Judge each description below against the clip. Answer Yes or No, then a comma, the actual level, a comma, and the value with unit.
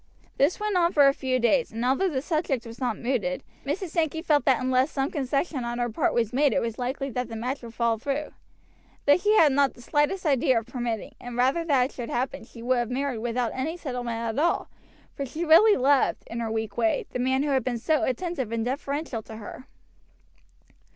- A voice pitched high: Yes, very high, 260 Hz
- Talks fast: Yes, fast, 225 wpm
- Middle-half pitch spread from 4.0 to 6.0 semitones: No, average, 3.6 semitones